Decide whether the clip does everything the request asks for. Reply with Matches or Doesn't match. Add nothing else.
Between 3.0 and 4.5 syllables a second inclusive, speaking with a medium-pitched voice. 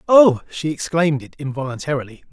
Doesn't match